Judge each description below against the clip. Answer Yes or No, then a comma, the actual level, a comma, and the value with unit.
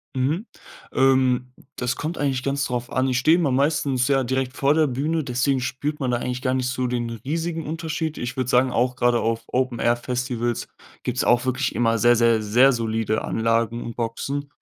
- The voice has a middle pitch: No, low, 125 Hz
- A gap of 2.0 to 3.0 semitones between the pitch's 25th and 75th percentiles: Yes, narrow, 2.5 semitones